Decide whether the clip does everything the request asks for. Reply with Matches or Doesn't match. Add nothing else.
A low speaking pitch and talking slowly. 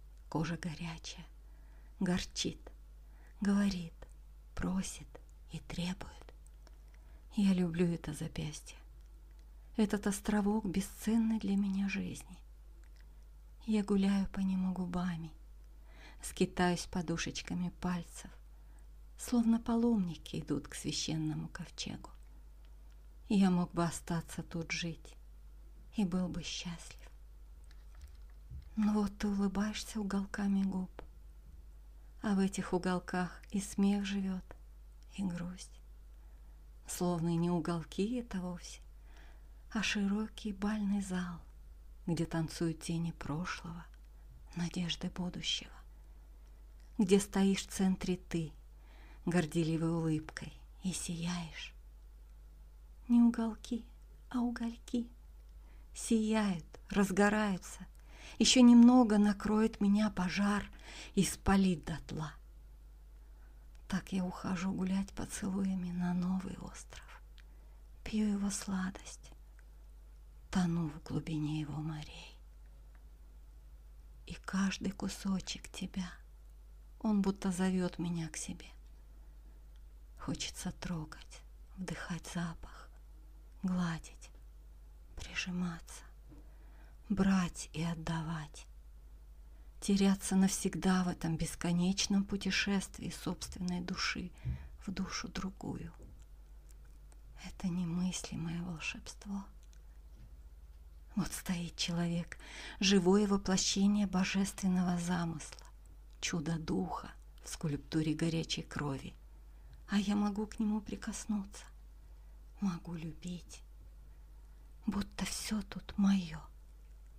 Doesn't match